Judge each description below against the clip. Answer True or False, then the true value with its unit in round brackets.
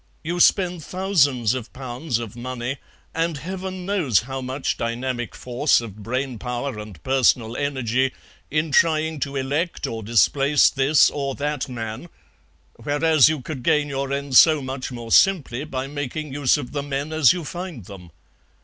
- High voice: False (135 Hz)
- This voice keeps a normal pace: True (160 wpm)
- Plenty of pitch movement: False (3.9 semitones)